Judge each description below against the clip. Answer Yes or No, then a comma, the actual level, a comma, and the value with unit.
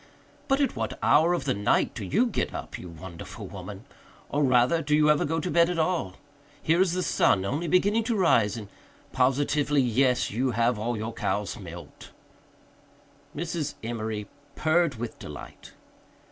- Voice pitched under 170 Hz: Yes, low, 135 Hz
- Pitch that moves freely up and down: Yes, wide, 7.4 semitones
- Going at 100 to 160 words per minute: No, average, 170 wpm